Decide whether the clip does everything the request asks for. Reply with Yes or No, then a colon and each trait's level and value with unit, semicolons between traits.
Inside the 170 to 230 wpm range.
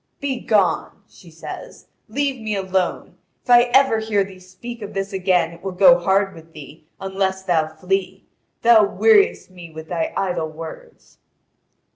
No: average, 155 wpm